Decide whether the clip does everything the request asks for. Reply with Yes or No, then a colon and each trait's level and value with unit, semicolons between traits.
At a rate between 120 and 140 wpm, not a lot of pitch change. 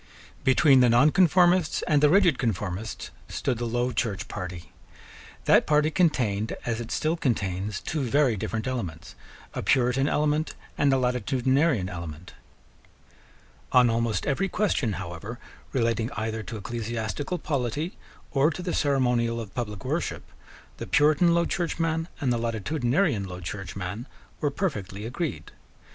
No: slow, 135 wpm; wide, 5.6 semitones